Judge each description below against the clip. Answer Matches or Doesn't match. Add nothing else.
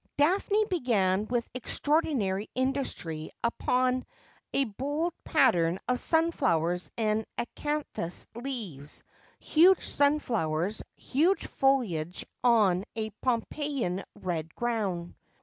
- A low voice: Doesn't match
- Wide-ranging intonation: Matches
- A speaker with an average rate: Doesn't match